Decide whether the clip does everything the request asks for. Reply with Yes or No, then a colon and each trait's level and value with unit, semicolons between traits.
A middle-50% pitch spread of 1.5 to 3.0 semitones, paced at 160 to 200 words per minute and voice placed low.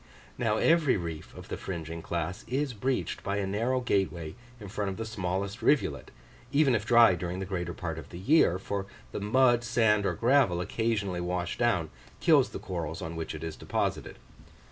No: average, 5.2 semitones; average, 190 wpm; low, 100 Hz